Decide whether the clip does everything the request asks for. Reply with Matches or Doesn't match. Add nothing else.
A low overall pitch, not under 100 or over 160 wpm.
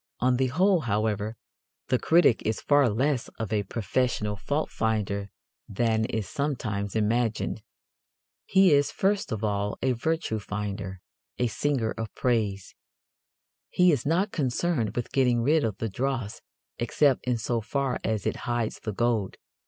Matches